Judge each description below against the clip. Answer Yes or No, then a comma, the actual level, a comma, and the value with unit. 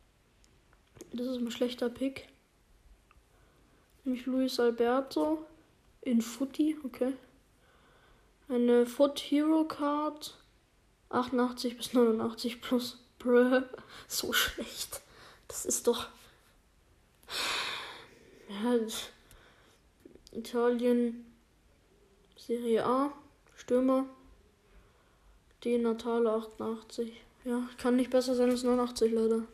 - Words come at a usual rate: No, slow, 85 wpm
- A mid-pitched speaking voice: No, high, 245 Hz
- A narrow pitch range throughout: Yes, narrow, 1.8 semitones